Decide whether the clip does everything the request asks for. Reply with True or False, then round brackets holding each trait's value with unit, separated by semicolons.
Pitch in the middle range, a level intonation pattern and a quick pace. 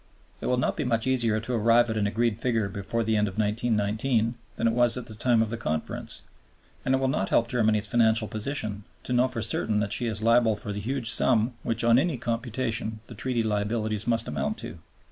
False (115 Hz; 2.1 semitones; 220 wpm)